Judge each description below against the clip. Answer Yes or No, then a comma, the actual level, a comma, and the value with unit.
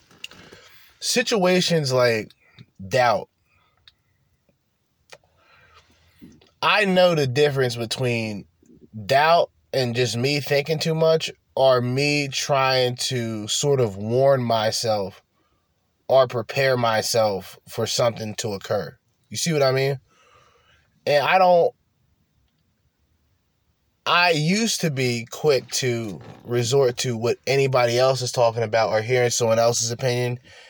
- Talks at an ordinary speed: No, slow, 110 wpm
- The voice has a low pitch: Yes, low, 125 Hz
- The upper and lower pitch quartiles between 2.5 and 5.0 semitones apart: Yes, average, 3.7 semitones